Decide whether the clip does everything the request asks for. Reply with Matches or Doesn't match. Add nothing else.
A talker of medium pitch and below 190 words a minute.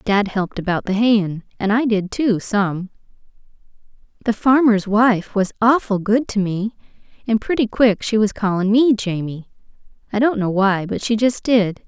Doesn't match